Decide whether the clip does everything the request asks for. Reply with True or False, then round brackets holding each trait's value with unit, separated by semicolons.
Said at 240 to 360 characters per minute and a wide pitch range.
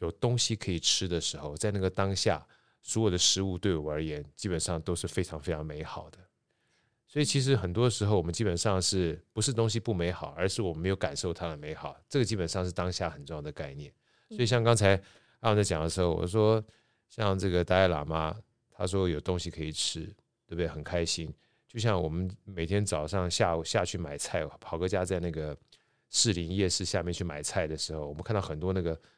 False (325 characters per minute; 4.6 semitones)